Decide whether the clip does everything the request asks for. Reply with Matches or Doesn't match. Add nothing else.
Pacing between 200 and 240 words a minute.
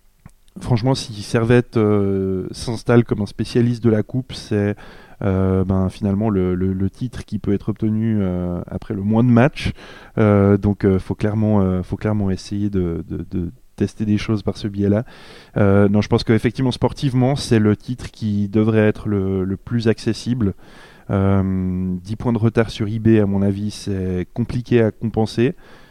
Doesn't match